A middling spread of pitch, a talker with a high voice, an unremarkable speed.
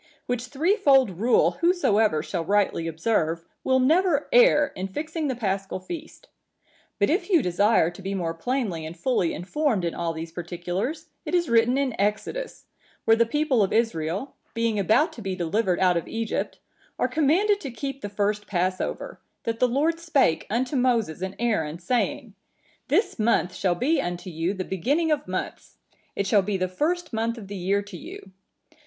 No: wide, 7.2 semitones; high, 220 Hz; average, 175 wpm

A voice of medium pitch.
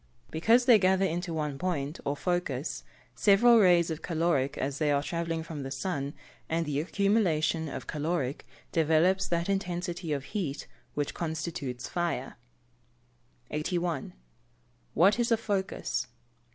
Yes: medium, 165 Hz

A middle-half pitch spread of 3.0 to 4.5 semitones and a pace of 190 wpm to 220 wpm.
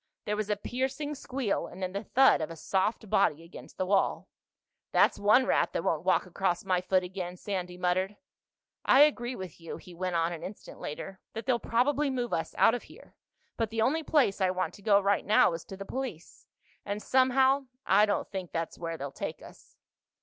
No: average, 5.1 semitones; fast, 205 wpm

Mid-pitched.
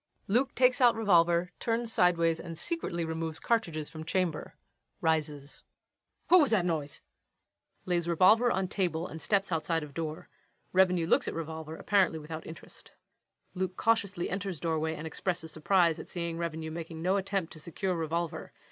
Yes: medium, 170 Hz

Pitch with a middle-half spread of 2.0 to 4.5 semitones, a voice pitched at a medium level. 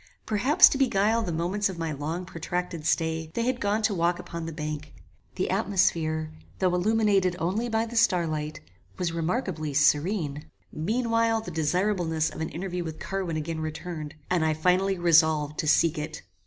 Yes: average, 4.1 semitones; medium, 175 Hz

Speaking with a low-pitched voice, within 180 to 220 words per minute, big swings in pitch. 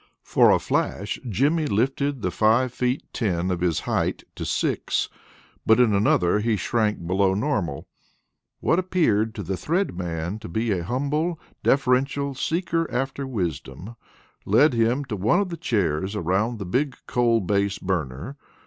No: low, 110 Hz; average, 155 wpm; wide, 6.3 semitones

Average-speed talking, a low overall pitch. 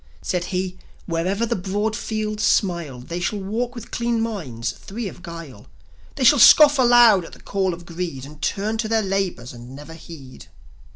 No: average, 180 wpm; high, 190 Hz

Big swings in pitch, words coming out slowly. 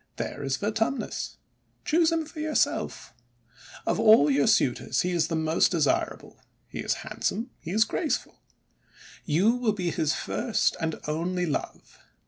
No: wide, 6.6 semitones; average, 150 wpm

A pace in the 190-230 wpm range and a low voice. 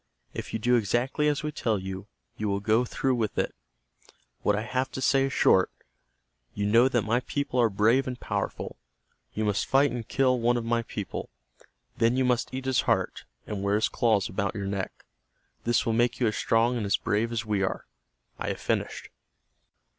Yes: average, 200 wpm; low, 115 Hz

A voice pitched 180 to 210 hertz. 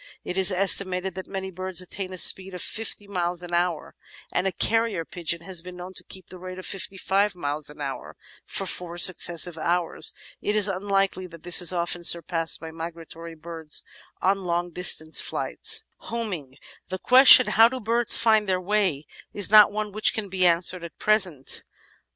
Yes: medium, 185 Hz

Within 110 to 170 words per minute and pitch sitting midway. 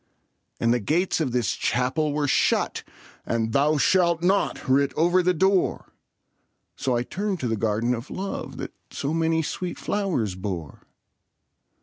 Yes: average, 150 wpm; medium, 145 Hz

